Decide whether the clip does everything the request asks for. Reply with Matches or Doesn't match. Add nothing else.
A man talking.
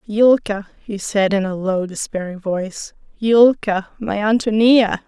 Doesn't match